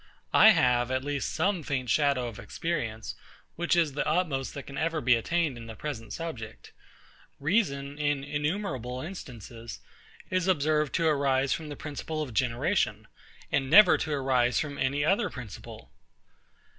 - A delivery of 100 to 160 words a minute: Yes, average, 155 wpm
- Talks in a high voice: No, medium, 140 Hz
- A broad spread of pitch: No, average, 4.1 semitones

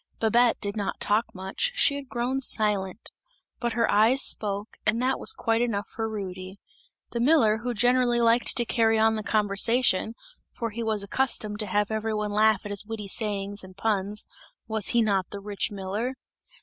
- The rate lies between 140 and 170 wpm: No, average, 185 wpm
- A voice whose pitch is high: Yes, high, 220 Hz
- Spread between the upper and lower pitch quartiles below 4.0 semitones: Yes, narrow, 2.6 semitones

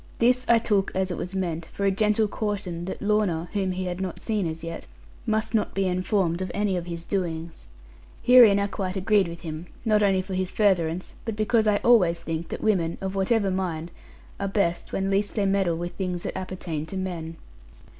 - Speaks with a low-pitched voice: No, high, 190 Hz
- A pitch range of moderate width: Yes, average, 3.1 semitones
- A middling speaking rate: No, fast, 210 wpm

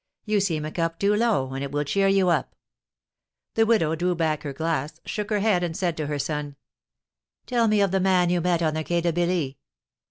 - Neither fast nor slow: No, fast, 225 wpm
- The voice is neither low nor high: Yes, medium, 175 Hz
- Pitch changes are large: No, average, 4.2 semitones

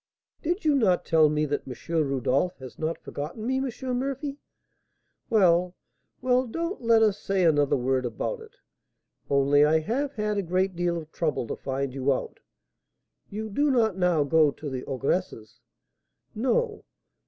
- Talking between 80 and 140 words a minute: No, average, 160 wpm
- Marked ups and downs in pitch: Yes, wide, 8.3 semitones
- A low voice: No, medium, 180 Hz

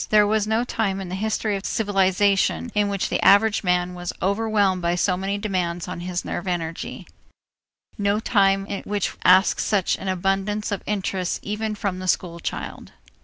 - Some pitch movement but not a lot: No, narrow, 2.3 semitones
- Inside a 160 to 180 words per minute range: Yes, average, 170 wpm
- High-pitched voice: Yes, high, 195 Hz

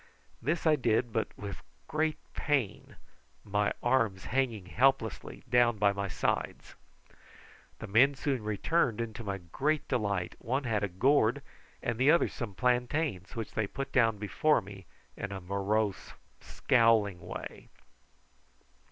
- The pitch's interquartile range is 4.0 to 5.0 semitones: Yes, average, 4.7 semitones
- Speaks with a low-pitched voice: Yes, low, 115 Hz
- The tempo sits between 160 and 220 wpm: No, average, 140 wpm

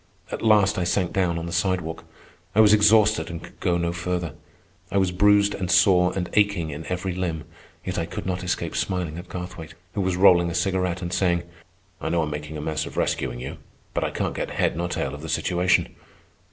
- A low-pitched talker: Yes, very low, 90 Hz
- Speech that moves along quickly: Yes, fast, 220 wpm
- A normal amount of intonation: No, narrow, 2.0 semitones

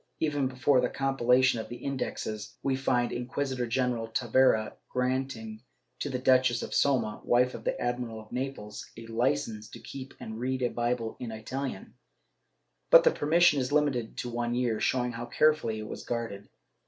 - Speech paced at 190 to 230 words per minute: No, average, 170 wpm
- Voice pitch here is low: Yes, low, 125 Hz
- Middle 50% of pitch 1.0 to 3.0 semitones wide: Yes, narrow, 2.5 semitones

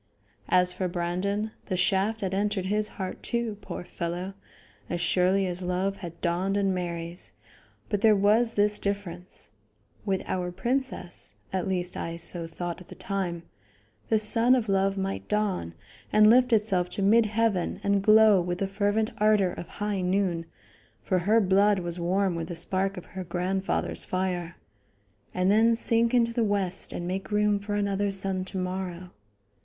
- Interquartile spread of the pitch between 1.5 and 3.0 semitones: Yes, narrow, 2.6 semitones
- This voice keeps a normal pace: Yes, average, 170 wpm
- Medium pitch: No, high, 195 Hz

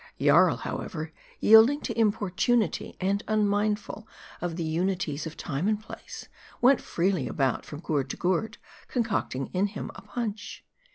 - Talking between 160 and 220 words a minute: No, average, 145 wpm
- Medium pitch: No, high, 200 Hz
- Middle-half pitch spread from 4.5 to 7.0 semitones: Yes, average, 4.8 semitones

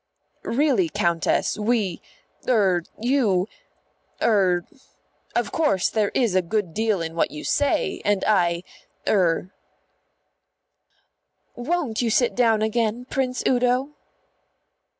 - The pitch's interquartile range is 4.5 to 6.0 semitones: Yes, average, 5.1 semitones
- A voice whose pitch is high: Yes, high, 215 Hz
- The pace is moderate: No, slow, 110 wpm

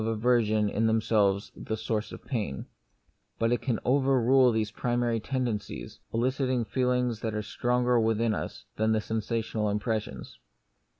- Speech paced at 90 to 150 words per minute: Yes, average, 145 wpm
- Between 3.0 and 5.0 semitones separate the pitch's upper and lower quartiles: No, narrow, 2.4 semitones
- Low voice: Yes, low, 115 Hz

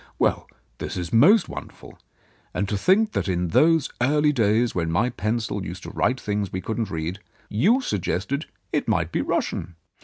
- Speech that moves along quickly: No, average, 175 wpm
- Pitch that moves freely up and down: Yes, wide, 7.2 semitones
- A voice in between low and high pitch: No, low, 110 Hz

